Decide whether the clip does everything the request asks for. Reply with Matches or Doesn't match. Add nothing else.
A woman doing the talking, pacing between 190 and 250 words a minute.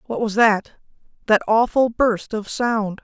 Doesn't match